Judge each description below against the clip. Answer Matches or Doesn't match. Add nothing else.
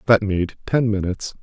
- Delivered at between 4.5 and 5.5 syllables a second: Matches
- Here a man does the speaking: Matches